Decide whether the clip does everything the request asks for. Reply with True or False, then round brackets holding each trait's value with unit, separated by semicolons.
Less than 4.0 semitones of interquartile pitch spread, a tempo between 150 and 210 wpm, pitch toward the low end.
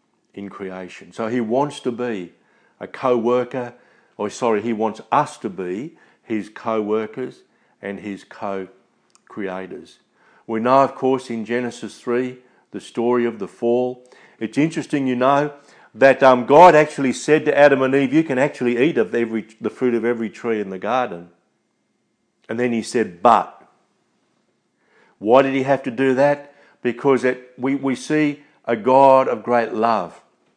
True (2.9 semitones; 165 wpm; 125 Hz)